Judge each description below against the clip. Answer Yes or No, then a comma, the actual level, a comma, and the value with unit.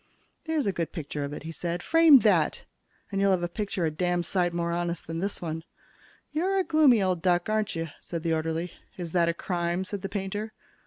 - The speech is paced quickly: Yes, fast, 220 wpm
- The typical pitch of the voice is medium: Yes, medium, 175 Hz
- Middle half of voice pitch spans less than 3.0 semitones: No, average, 3.3 semitones